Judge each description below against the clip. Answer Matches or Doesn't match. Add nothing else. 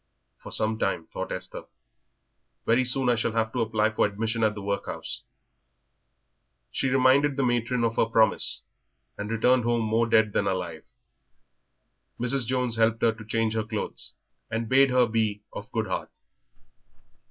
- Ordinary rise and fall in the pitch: Doesn't match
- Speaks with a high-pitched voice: Doesn't match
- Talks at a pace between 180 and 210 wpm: Doesn't match